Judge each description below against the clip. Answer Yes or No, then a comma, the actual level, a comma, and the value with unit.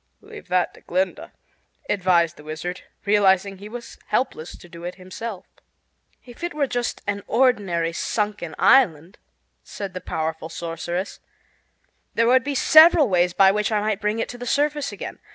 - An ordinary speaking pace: Yes, average, 165 wpm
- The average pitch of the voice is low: No, high, 200 Hz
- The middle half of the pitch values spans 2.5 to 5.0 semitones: No, wide, 5.5 semitones